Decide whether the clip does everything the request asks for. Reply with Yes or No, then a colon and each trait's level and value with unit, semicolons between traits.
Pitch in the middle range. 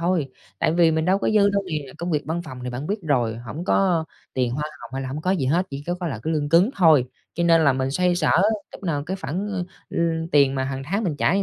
Yes: medium, 160 Hz